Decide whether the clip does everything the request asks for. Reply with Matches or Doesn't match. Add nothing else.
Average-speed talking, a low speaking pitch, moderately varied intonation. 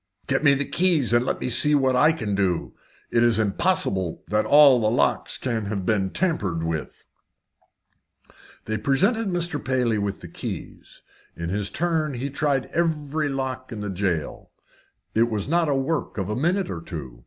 Doesn't match